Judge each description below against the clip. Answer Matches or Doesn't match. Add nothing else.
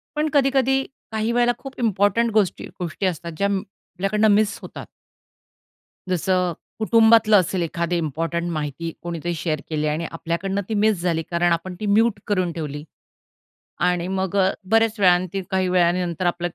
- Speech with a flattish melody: Doesn't match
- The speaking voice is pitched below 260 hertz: Matches